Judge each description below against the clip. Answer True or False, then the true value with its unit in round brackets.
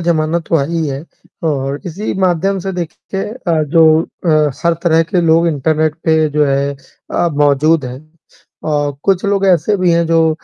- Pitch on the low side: False (160 Hz)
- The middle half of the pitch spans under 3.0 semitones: True (2.5 semitones)